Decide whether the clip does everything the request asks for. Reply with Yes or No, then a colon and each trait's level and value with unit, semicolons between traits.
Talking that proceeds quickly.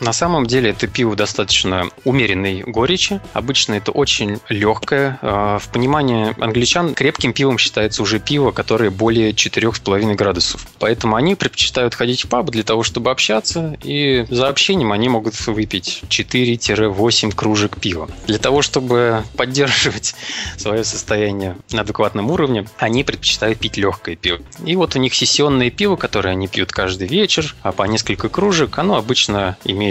No: average, 150 wpm